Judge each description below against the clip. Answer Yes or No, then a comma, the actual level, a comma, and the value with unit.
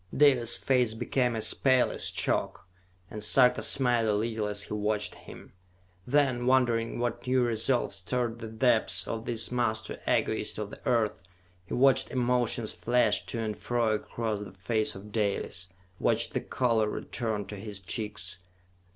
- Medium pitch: No, low, 115 Hz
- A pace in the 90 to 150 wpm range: No, average, 160 wpm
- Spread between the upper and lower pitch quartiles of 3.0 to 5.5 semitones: No, narrow, 2.5 semitones